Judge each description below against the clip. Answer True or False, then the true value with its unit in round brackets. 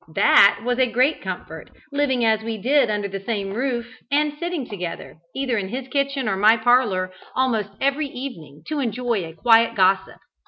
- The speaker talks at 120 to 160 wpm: False (180 wpm)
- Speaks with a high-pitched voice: True (235 Hz)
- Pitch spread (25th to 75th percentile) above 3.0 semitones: True (4.9 semitones)